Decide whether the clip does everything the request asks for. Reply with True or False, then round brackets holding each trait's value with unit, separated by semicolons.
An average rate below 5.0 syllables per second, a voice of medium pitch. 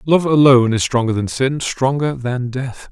False (4.6 syllables/s; 130 Hz)